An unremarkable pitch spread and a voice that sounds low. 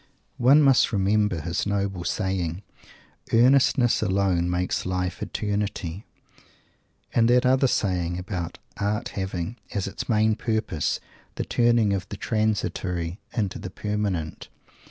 Yes: average, 3.2 semitones; low, 100 Hz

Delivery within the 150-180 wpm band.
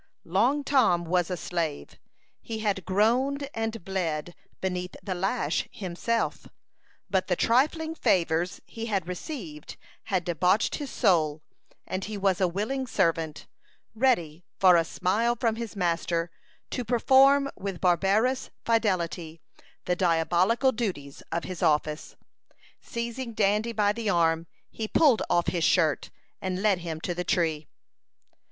No: slow, 135 wpm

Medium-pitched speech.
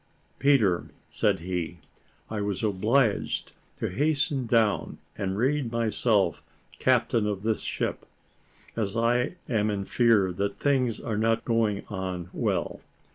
No: low, 110 Hz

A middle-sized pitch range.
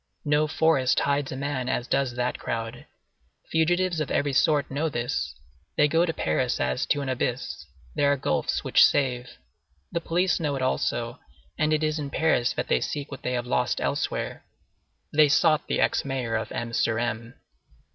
Yes: average, 3.9 semitones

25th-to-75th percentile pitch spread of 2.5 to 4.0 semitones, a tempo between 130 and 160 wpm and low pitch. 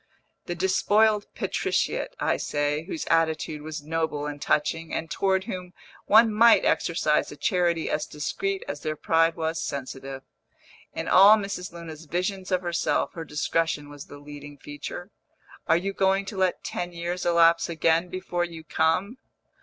No: average, 3.6 semitones; average, 155 wpm; medium, 170 Hz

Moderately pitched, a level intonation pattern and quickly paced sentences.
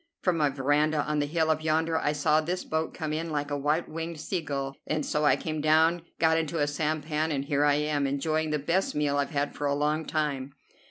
Yes: medium, 150 Hz; narrow, 1.6 semitones; fast, 235 wpm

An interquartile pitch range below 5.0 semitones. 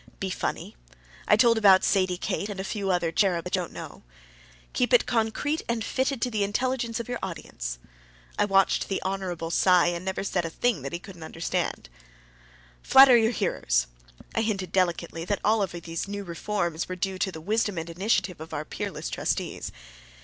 Yes: average, 4.2 semitones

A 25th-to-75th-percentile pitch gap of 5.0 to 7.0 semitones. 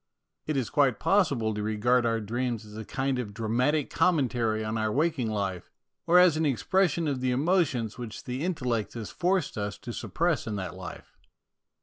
Yes: wide, 5.6 semitones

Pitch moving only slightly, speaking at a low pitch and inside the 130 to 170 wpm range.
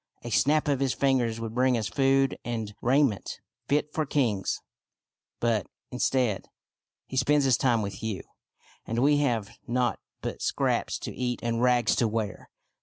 No: average, 3.2 semitones; low, 125 Hz; average, 165 wpm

